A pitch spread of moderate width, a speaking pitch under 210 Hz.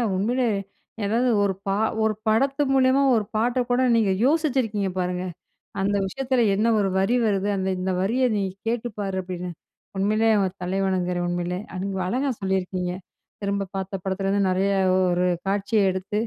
Yes: average, 3.5 semitones; high, 200 Hz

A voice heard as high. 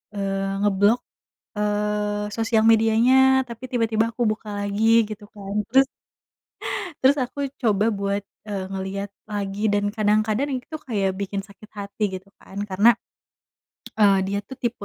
Yes: high, 210 Hz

